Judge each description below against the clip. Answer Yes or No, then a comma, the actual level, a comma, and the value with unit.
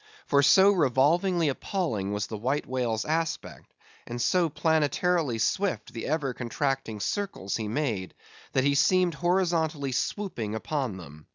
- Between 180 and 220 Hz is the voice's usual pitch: No, medium, 140 Hz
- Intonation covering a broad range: Yes, wide, 6.6 semitones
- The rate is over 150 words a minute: No, average, 140 wpm